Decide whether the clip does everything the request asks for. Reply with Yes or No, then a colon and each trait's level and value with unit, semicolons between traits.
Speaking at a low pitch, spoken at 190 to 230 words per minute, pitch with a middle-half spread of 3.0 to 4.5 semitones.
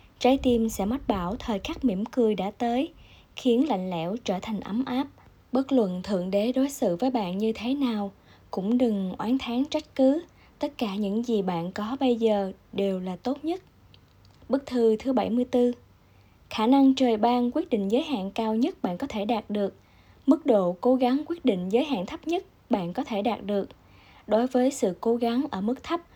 No: high, 240 Hz; average, 205 wpm; average, 4.2 semitones